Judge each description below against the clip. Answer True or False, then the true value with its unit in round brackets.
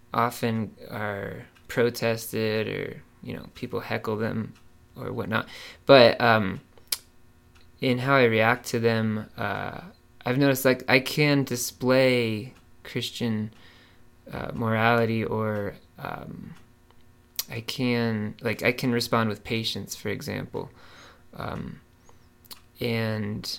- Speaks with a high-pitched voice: False (115 Hz)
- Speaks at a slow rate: True (110 wpm)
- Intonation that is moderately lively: False (1.8 semitones)